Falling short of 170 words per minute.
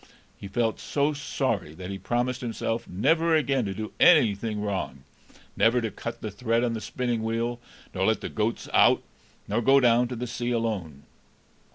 No: average, 180 wpm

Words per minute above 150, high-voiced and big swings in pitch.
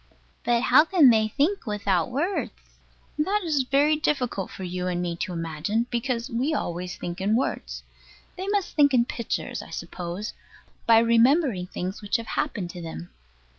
Yes: average, 170 wpm; high, 230 Hz; wide, 7.6 semitones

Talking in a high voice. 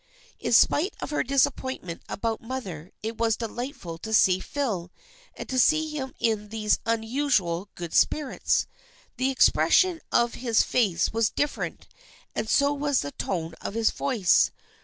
Yes: high, 230 Hz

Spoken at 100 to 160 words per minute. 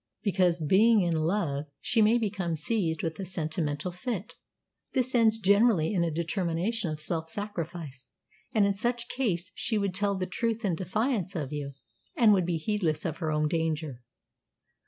No: average, 170 wpm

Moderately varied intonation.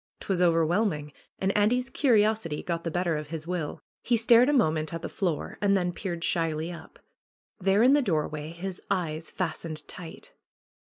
Yes: average, 4.3 semitones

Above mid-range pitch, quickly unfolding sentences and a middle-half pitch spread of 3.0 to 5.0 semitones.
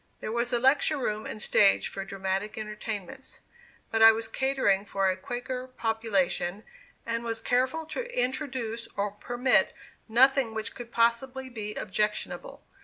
No: high, 230 Hz; average, 145 wpm; average, 3.3 semitones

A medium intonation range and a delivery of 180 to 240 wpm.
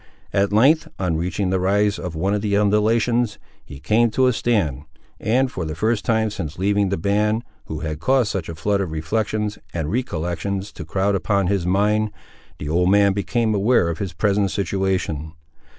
Yes: average, 3.3 semitones; average, 185 wpm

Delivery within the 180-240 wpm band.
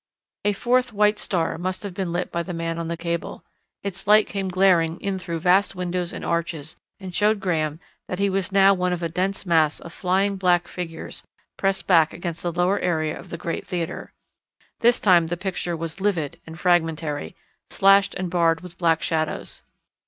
Yes: average, 190 wpm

